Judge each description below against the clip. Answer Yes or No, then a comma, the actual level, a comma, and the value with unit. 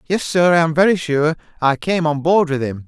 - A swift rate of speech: Yes, fast, 250 wpm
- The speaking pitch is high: No, medium, 160 Hz